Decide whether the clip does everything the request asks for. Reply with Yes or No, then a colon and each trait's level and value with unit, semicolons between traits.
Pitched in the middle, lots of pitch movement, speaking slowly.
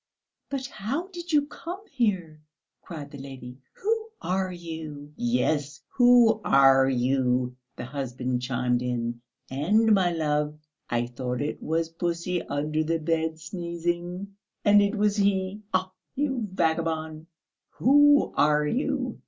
Yes: medium, 165 Hz; wide, 6.7 semitones; slow, 130 wpm